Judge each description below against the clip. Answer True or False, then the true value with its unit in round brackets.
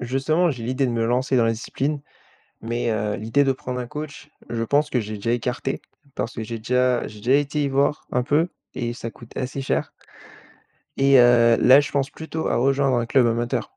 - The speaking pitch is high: False (125 Hz)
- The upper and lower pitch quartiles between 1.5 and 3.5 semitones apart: True (2.9 semitones)